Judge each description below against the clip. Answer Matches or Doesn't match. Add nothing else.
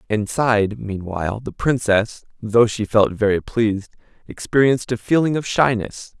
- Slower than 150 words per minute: Matches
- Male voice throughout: Matches